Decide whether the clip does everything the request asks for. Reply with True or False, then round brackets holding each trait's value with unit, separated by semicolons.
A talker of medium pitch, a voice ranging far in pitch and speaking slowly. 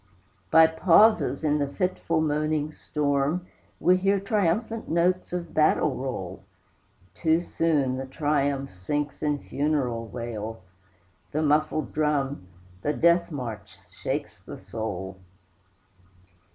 False (150 Hz; 4.1 semitones; 110 wpm)